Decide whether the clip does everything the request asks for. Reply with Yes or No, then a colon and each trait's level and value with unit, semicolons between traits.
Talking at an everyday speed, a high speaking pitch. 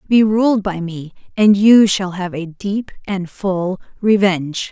Yes: average, 165 wpm; high, 195 Hz